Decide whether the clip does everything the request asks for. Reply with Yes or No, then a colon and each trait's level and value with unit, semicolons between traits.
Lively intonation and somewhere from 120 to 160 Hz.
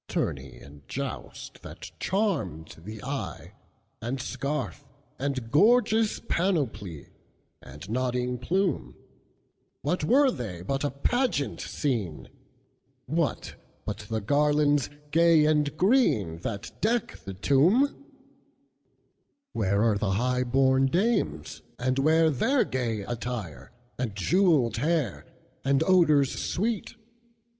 Yes: wide, 7.2 semitones; low, 135 Hz